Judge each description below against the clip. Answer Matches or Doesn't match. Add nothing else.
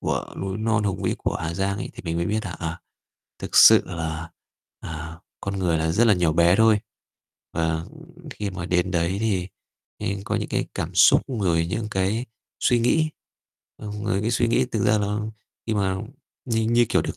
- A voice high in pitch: Doesn't match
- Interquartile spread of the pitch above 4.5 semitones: Doesn't match